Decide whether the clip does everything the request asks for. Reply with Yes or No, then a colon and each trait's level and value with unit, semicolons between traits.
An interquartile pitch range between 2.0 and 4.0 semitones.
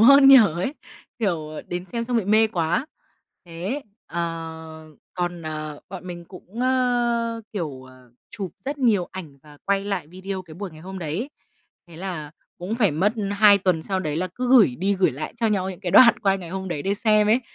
No: average, 4.8 semitones